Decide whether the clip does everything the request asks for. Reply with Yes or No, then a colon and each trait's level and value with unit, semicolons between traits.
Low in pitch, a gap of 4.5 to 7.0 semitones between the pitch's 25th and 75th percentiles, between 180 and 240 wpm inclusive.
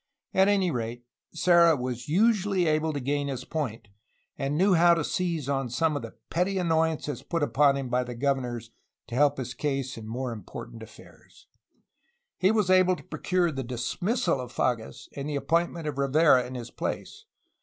No: medium, 145 Hz; wide, 5.4 semitones; average, 185 wpm